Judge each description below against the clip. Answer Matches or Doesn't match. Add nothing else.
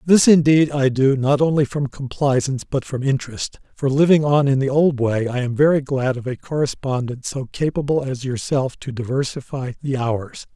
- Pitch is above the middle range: Doesn't match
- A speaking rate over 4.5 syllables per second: Matches